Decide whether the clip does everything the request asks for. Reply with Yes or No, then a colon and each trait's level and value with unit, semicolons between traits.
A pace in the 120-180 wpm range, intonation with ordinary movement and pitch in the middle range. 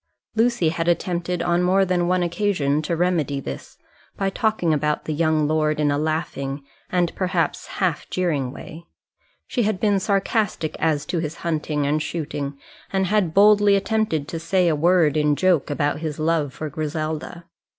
Yes: average, 170 wpm; average, 3.4 semitones; medium, 165 Hz